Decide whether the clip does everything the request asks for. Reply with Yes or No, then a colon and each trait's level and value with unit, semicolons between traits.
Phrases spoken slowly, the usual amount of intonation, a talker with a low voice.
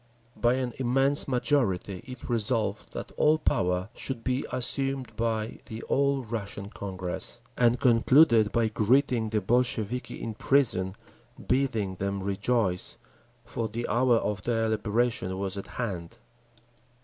Yes: slow, 130 wpm; average, 3.9 semitones; low, 115 Hz